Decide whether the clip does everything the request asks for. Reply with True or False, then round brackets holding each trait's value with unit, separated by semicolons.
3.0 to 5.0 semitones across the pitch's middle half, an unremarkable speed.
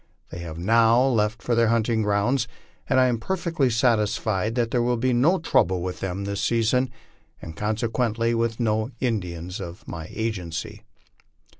True (3.3 semitones; 160 wpm)